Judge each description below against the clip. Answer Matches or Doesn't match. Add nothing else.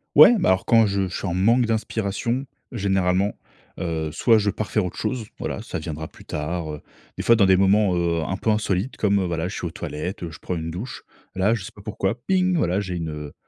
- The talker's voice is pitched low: Matches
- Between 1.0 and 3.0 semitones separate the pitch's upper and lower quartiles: Doesn't match